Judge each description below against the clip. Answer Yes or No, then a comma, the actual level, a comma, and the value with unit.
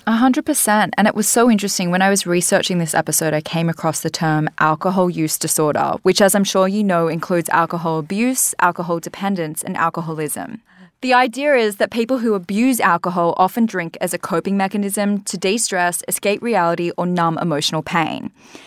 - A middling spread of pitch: Yes, average, 3.9 semitones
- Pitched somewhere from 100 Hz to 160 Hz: No, medium, 185 Hz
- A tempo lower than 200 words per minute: Yes, average, 180 wpm